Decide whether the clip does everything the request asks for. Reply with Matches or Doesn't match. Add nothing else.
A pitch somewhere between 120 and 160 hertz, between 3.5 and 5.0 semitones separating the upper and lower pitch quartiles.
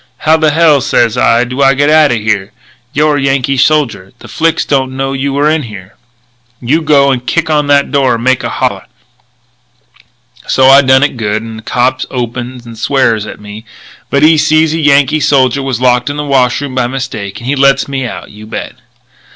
Doesn't match